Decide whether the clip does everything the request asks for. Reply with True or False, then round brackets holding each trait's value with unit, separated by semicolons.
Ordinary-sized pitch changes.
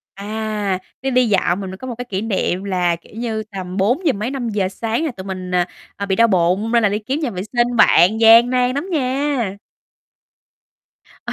True (4.3 semitones)